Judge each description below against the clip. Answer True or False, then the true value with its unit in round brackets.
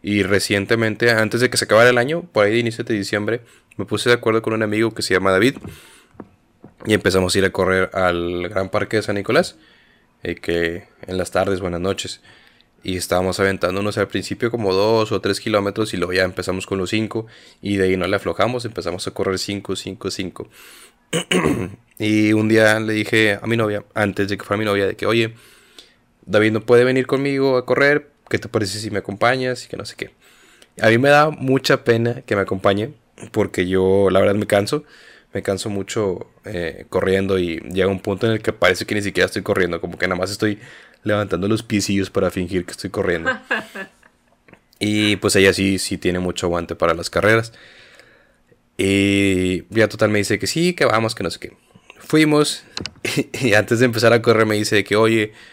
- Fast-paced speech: True (205 wpm)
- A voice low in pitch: True (105 Hz)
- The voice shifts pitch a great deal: False (2.8 semitones)